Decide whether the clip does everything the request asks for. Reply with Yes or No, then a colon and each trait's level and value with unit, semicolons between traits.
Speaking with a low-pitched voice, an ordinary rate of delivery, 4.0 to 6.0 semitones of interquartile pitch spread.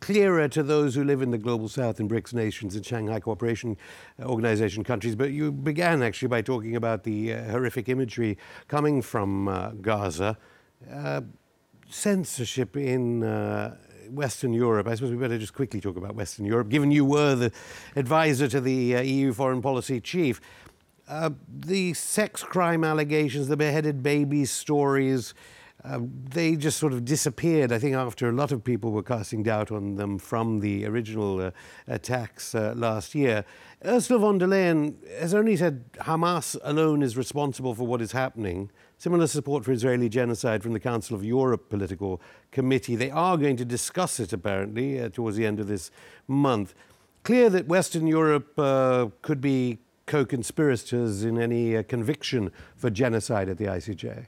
Yes: low, 125 Hz; average, 170 wpm; average, 4.7 semitones